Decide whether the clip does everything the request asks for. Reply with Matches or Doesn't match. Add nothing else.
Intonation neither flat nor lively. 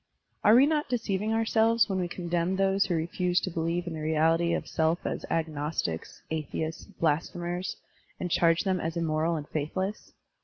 Matches